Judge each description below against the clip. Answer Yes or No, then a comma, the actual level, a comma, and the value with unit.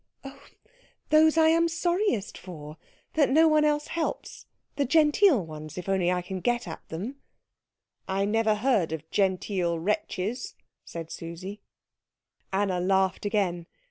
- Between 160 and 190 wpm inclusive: No, average, 140 wpm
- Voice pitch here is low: No, high, 205 Hz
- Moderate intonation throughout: No, wide, 8.8 semitones